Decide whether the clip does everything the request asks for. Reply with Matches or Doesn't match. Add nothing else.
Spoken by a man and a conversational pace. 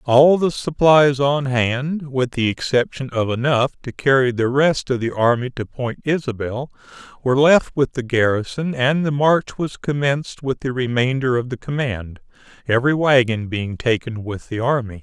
Matches